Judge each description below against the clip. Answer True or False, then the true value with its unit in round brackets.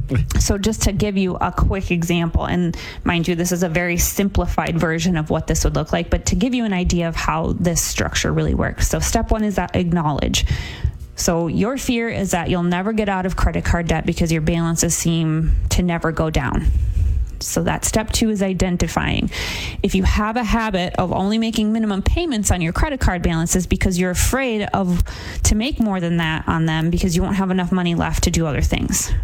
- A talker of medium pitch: True (175 Hz)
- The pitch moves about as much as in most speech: True (4.1 semitones)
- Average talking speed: False (215 wpm)